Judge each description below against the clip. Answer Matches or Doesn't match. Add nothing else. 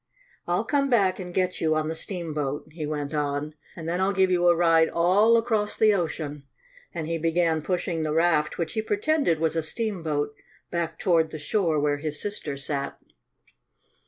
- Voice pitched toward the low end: Doesn't match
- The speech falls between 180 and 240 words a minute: Matches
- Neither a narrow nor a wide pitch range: Matches